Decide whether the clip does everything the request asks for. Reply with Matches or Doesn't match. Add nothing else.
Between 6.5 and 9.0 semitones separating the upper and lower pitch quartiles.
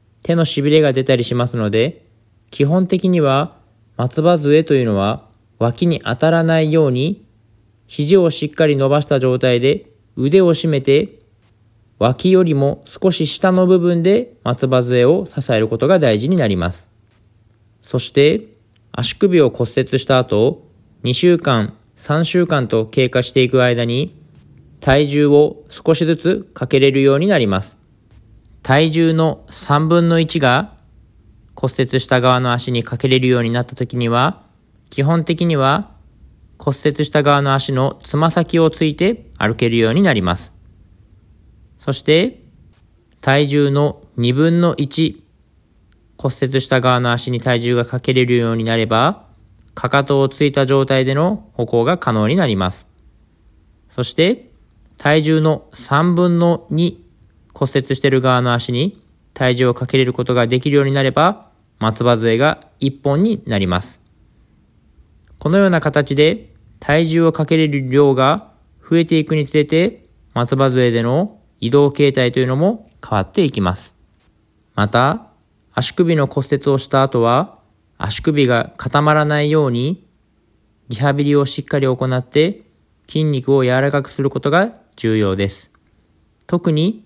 Doesn't match